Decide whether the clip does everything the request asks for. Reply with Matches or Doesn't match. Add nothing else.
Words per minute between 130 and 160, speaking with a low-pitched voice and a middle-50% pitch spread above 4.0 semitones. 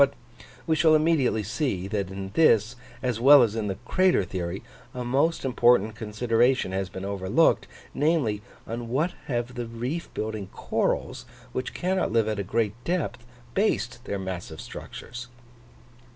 Matches